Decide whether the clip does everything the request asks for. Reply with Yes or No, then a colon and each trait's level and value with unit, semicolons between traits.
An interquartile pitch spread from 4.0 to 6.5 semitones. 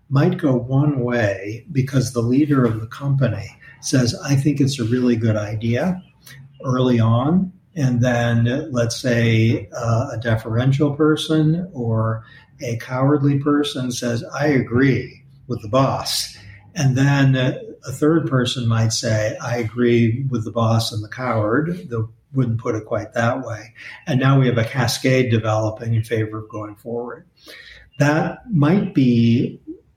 No: average, 3.3 semitones